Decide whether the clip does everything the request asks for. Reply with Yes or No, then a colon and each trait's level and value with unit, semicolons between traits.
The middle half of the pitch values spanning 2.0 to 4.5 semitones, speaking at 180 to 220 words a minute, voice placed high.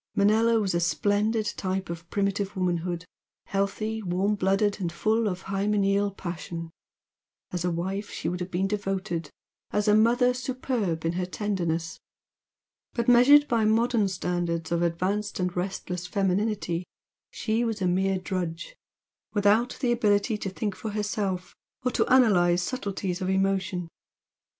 No: average, 3.1 semitones; average, 145 wpm; high, 195 Hz